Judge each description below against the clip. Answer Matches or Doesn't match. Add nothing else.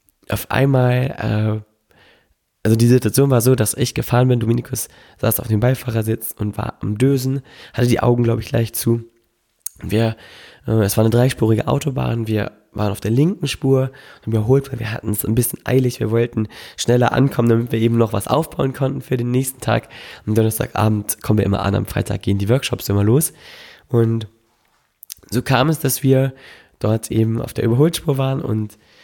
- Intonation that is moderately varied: Matches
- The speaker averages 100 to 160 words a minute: Doesn't match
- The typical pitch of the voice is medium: Doesn't match